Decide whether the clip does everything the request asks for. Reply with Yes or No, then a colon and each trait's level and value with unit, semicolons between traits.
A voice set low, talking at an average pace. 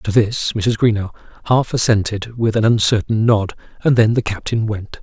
Yes: low, 110 Hz; average, 180 wpm